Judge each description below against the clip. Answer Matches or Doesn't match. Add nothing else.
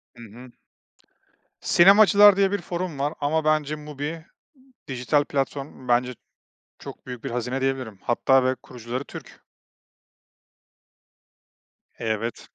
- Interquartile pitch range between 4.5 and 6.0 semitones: Doesn't match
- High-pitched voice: Doesn't match